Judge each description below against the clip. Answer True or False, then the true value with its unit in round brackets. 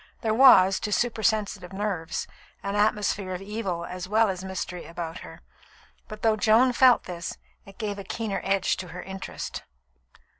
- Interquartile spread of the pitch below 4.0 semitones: True (2.8 semitones)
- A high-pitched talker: True (200 Hz)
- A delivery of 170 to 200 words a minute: False (160 wpm)